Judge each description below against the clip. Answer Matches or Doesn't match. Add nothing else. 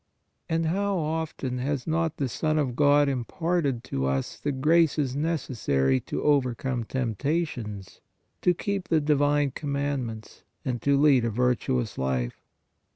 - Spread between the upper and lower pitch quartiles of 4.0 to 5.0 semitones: Matches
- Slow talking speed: Doesn't match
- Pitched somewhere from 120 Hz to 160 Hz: Matches